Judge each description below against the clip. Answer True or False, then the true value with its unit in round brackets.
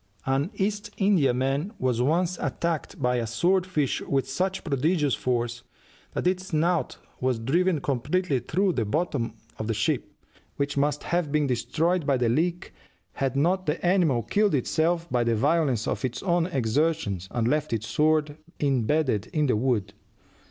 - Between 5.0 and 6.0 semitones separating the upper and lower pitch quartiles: True (5.6 semitones)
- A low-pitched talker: False (145 Hz)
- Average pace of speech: True (160 wpm)